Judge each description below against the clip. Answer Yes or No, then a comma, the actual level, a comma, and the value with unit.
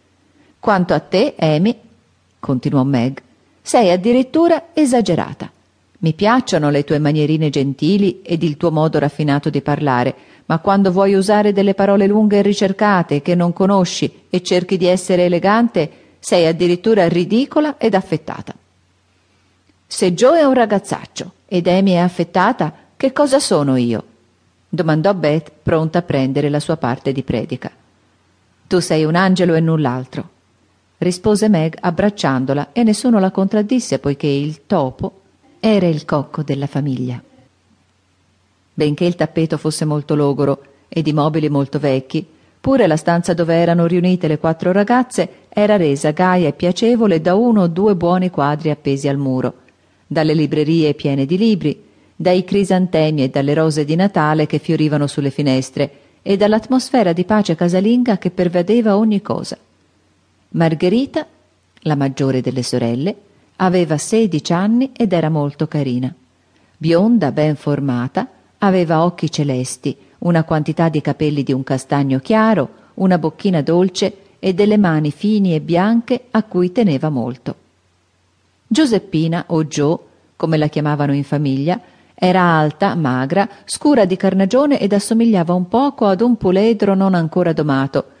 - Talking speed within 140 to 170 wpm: Yes, average, 145 wpm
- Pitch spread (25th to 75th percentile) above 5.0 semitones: Yes, wide, 5.6 semitones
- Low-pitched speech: No, medium, 165 Hz